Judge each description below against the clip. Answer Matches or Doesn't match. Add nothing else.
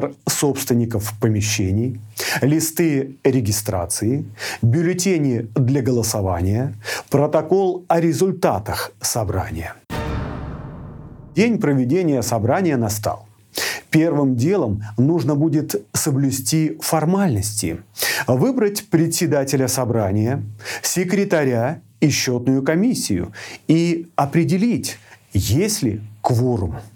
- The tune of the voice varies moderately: Doesn't match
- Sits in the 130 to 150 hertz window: Matches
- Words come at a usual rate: Doesn't match